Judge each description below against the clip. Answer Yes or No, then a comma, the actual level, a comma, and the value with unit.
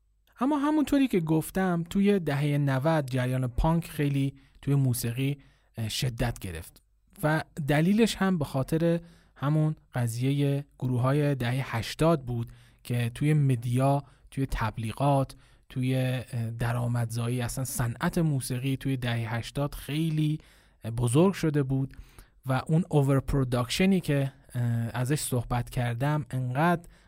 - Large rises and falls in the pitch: No, average, 4.0 semitones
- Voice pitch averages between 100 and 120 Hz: No, low, 135 Hz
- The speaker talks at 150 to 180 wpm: No, average, 115 wpm